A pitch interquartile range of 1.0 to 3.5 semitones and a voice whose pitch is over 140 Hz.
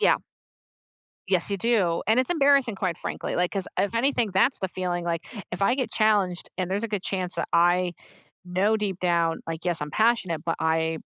No: average, 4.0 semitones; medium, 185 Hz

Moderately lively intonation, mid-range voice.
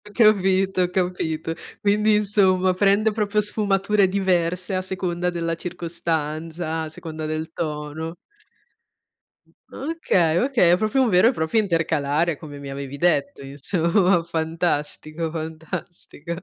Yes: average, 3.5 semitones; medium, 175 Hz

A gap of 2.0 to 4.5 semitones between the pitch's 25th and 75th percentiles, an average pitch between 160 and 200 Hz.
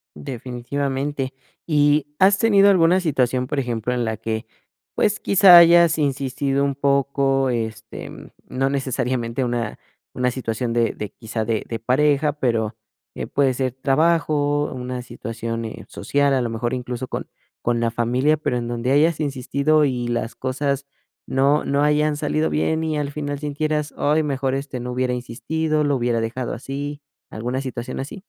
No: average, 3.5 semitones; low, 135 Hz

